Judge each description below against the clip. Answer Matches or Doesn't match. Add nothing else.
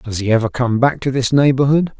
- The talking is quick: Matches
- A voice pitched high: Doesn't match